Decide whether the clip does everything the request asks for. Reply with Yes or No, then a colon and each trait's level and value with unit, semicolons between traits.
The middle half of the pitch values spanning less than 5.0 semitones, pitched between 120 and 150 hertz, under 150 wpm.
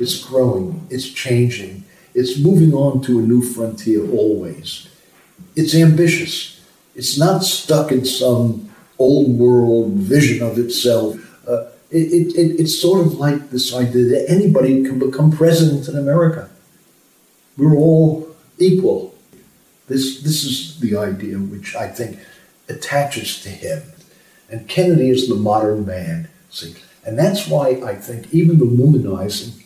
No: wide, 5.4 semitones; medium, 140 Hz; average, 140 wpm